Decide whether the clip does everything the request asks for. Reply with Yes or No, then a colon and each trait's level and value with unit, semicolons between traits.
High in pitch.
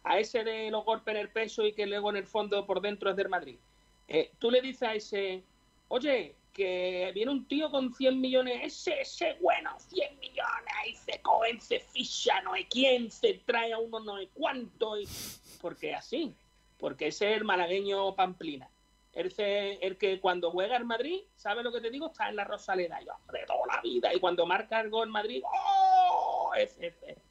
Yes: high, 225 Hz